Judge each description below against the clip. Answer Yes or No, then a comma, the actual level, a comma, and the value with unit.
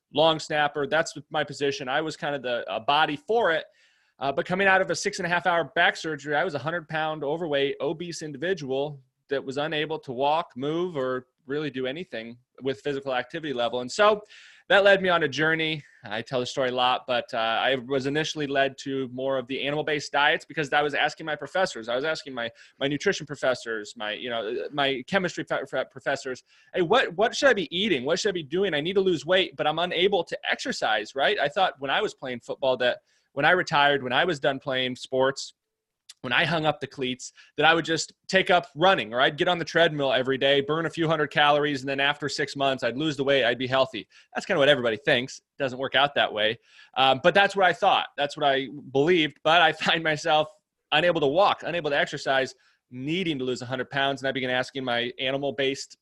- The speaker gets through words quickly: Yes, fast, 230 wpm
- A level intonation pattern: No, average, 3.6 semitones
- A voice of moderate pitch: Yes, medium, 145 Hz